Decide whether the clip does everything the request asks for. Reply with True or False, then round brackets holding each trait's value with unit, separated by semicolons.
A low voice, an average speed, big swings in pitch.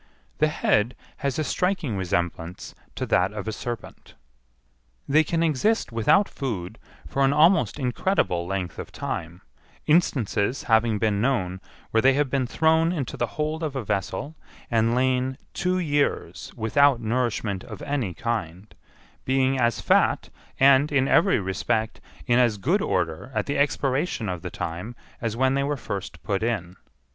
True (120 Hz; 155 wpm; 5.7 semitones)